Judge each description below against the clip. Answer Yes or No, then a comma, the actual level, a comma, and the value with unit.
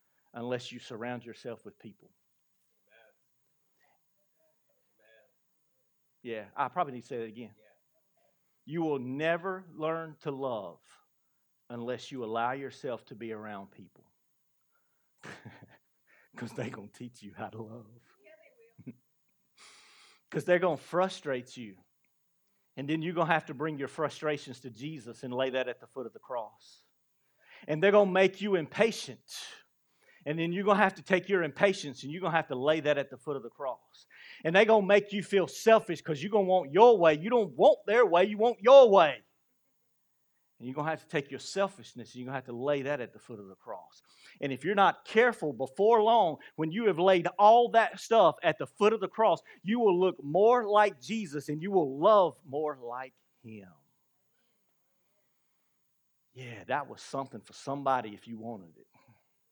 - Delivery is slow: No, average, 185 wpm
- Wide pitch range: Yes, wide, 7.7 semitones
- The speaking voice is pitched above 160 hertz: No, medium, 155 Hz